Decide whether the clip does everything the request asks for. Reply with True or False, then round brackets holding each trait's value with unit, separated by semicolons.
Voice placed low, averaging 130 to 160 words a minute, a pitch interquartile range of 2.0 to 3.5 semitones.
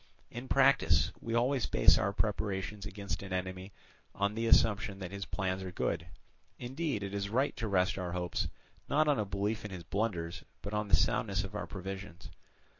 False (100 Hz; 190 wpm; 3.0 semitones)